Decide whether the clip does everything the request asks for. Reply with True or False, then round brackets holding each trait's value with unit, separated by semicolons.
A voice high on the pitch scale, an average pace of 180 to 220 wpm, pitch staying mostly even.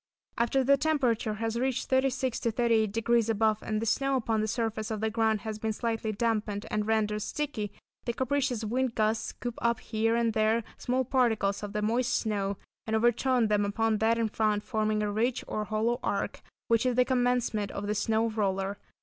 True (225 Hz; 190 wpm; 2.0 semitones)